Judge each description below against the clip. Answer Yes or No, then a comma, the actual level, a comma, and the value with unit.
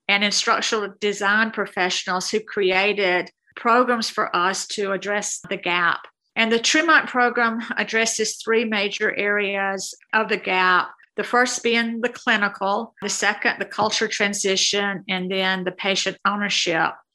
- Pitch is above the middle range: Yes, high, 205 Hz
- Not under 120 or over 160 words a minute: Yes, slow, 135 wpm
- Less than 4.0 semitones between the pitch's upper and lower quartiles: Yes, narrow, 2.4 semitones